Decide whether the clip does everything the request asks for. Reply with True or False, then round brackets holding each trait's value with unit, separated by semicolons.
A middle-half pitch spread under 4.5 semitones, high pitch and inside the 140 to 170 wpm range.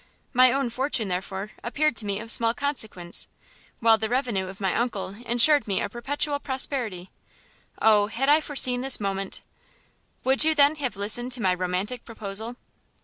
False (5.0 semitones; 230 Hz; 165 wpm)